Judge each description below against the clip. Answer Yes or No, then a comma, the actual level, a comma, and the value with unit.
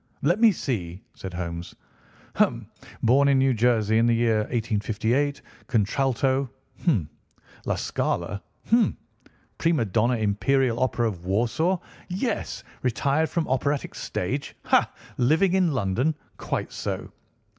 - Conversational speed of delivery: No, slow, 110 wpm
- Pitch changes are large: No, average, 4.9 semitones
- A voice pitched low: Yes, low, 125 Hz